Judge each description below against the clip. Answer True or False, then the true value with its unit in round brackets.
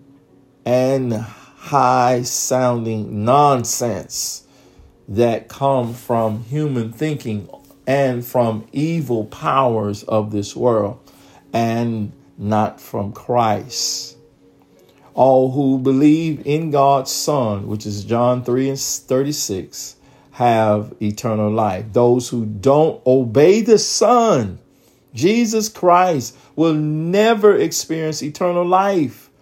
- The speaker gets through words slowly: True (95 wpm)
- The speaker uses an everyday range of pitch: True (4.8 semitones)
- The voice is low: True (125 Hz)